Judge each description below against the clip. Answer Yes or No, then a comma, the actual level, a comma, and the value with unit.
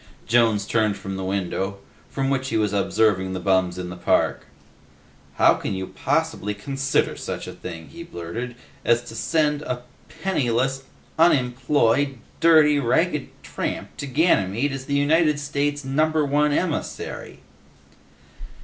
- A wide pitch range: Yes, wide, 6.3 semitones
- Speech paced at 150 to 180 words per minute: No, average, 140 wpm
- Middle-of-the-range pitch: No, low, 130 Hz